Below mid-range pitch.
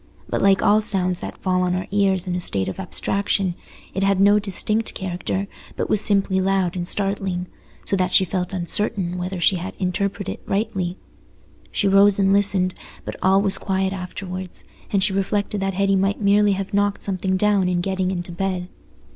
No: high, 190 Hz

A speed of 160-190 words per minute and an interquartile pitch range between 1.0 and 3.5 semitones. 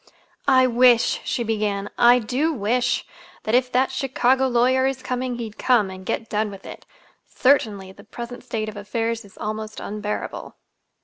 Yes: average, 165 wpm; average, 3.1 semitones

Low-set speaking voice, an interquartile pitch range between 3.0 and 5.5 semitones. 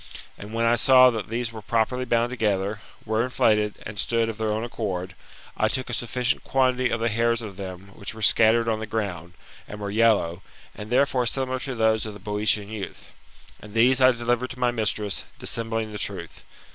No: low, 110 Hz; narrow, 2.5 semitones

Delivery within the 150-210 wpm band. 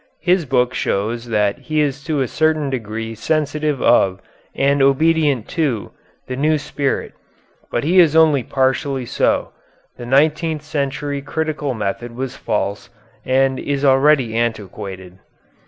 No: slow, 135 wpm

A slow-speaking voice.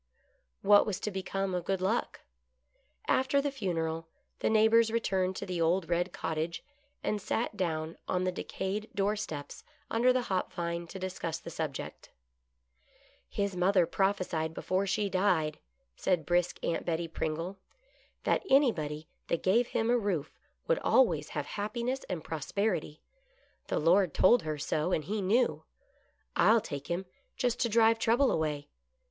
No: average, 155 wpm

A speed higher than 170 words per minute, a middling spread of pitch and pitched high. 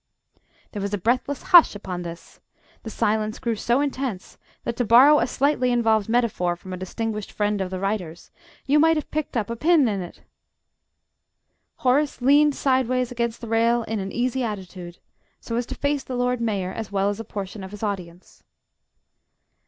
Yes: average, 185 wpm; average, 4.2 semitones; high, 225 Hz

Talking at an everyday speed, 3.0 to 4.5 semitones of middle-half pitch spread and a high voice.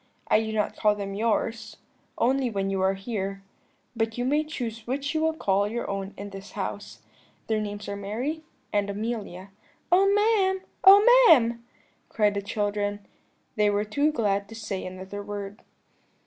Yes: average, 165 wpm; average, 3.8 semitones; high, 215 Hz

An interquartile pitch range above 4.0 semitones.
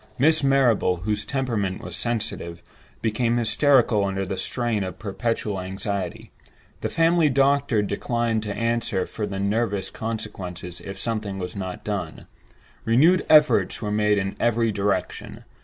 No: average, 3.5 semitones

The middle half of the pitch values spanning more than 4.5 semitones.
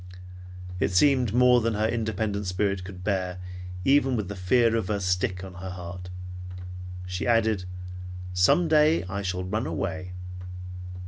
No: average, 3.9 semitones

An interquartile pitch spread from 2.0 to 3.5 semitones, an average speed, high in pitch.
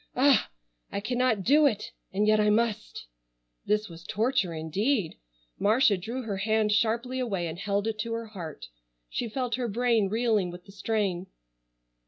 Yes: average, 3.1 semitones; average, 165 wpm; high, 215 Hz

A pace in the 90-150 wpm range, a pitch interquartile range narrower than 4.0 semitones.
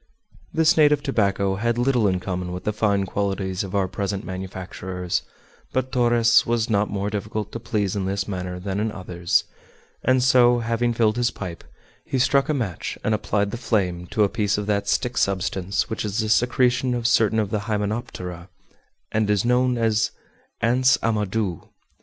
No: average, 175 wpm; average, 3.6 semitones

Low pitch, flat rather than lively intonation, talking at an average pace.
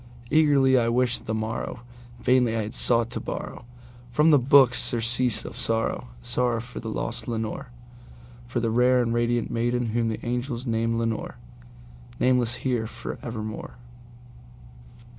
No: low, 120 Hz; narrow, 1.6 semitones; slow, 125 wpm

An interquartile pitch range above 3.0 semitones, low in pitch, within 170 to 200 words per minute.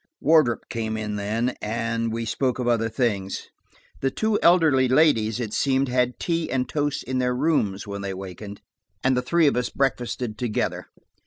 Yes: average, 3.5 semitones; low, 125 Hz; average, 175 wpm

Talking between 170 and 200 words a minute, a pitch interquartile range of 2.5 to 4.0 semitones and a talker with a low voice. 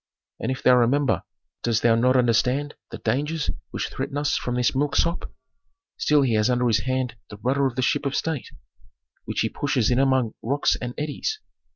Yes: average, 190 wpm; average, 3.1 semitones; low, 130 Hz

